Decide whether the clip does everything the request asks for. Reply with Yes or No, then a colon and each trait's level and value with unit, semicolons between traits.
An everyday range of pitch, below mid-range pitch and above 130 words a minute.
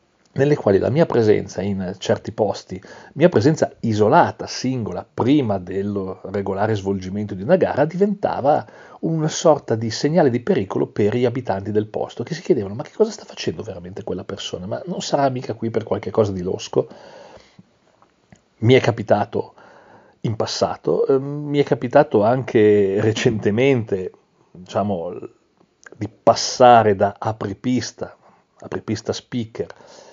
No: wide, 6.0 semitones; low, 120 Hz; average, 140 wpm